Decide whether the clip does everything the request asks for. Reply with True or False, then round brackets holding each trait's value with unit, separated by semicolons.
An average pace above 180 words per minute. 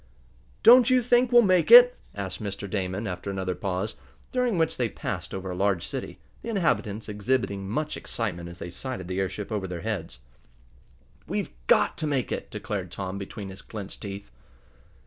False (175 wpm)